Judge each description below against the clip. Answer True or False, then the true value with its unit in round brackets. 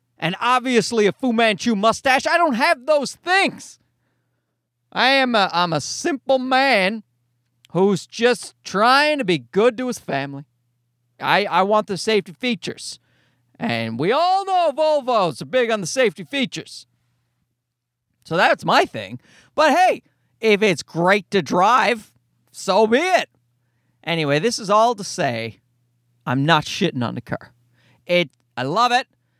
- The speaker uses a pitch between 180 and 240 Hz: True (190 Hz)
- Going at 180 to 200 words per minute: False (150 wpm)